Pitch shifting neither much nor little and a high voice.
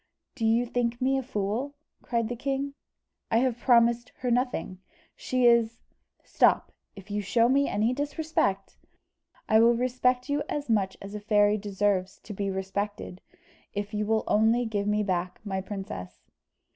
Yes: average, 3.4 semitones; high, 225 Hz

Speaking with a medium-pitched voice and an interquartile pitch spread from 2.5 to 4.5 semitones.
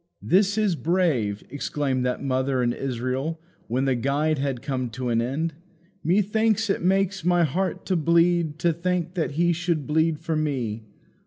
No: medium, 155 Hz; average, 5.2 semitones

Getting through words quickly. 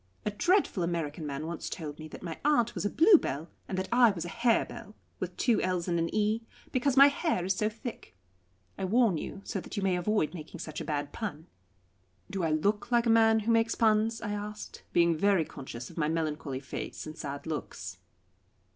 Yes: fast, 210 wpm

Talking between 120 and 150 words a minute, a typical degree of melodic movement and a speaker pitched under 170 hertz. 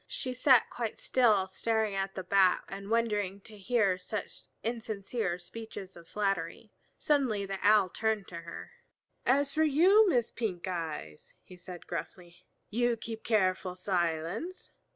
No: average, 145 wpm; average, 4.0 semitones; high, 205 Hz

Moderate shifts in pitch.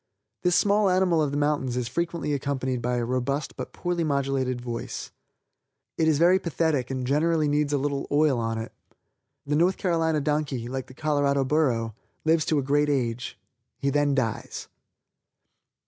Yes: average, 3.4 semitones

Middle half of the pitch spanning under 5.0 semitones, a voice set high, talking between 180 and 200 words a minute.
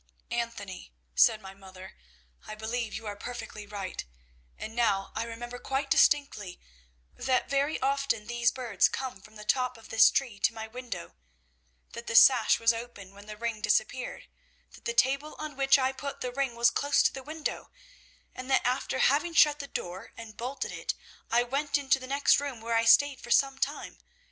Yes: average, 3.8 semitones; high, 240 Hz; average, 190 wpm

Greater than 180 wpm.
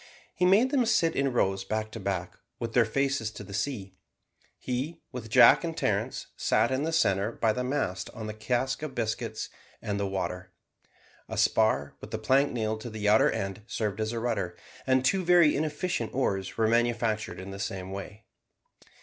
Yes: average, 190 wpm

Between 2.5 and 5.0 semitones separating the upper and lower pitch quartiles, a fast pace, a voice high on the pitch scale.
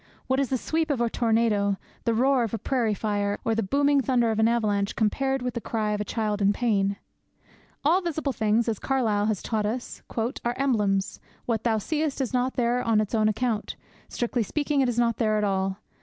Yes: average, 3.3 semitones; fast, 210 wpm; high, 230 Hz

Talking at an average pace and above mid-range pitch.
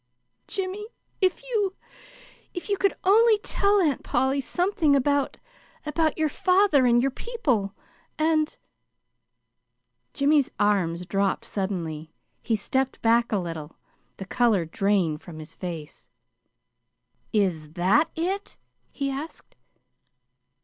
No: slow, 115 wpm; very high, 265 Hz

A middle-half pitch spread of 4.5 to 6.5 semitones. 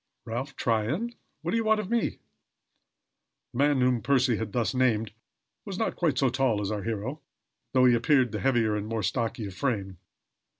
No: average, 3.8 semitones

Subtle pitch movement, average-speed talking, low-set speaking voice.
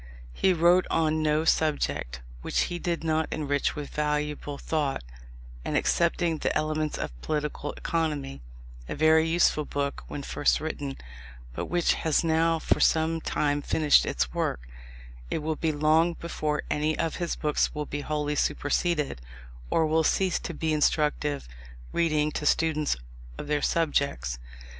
No: narrow, 1.7 semitones; average, 150 wpm; medium, 155 Hz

